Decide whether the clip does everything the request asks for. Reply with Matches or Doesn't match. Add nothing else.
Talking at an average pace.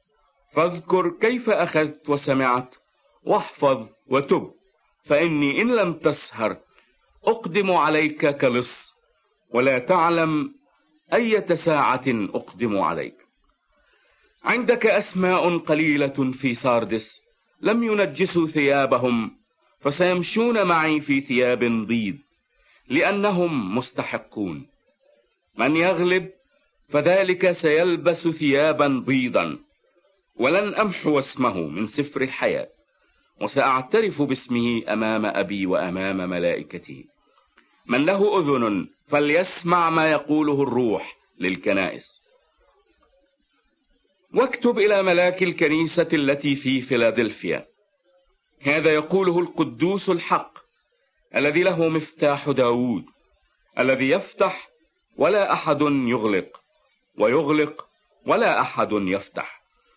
Doesn't match